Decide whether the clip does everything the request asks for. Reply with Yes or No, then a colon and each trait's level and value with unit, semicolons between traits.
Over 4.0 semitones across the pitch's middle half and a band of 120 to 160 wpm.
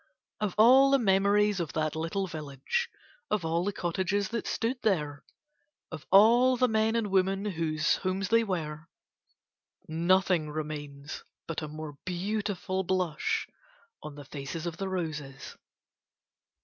Yes: average, 5.0 semitones; slow, 135 wpm